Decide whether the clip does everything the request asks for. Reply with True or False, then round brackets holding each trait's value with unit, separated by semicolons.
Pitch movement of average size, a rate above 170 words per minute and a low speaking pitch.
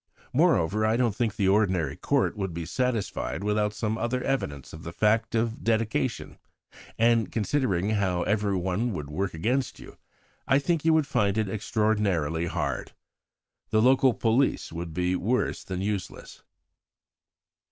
False (4.2 semitones; 145 wpm; 105 Hz)